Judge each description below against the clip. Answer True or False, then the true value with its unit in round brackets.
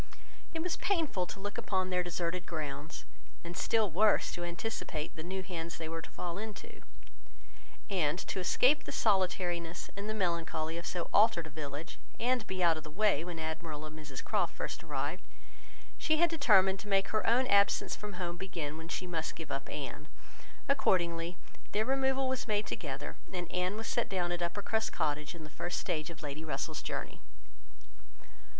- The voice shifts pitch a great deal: False (4.2 semitones)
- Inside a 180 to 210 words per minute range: True (185 wpm)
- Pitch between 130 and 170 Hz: False (180 Hz)